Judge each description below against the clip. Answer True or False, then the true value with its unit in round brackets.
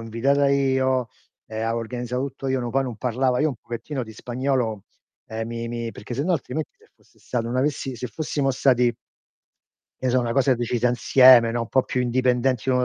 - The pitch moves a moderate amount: False (2.1 semitones)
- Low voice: True (125 Hz)